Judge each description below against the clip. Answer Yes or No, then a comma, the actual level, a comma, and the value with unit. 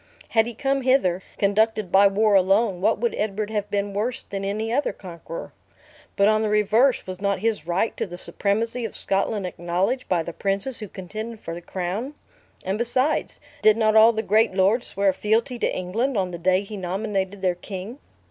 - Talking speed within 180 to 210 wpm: Yes, average, 195 wpm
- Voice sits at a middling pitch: No, high, 205 Hz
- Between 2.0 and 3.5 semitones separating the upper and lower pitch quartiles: Yes, average, 3.0 semitones